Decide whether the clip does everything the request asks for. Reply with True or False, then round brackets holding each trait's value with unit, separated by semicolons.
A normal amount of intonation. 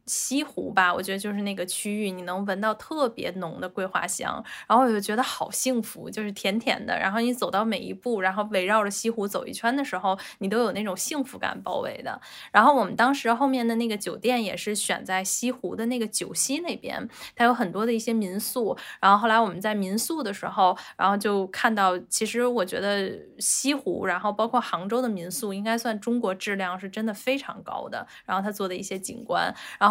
True (3.7 semitones)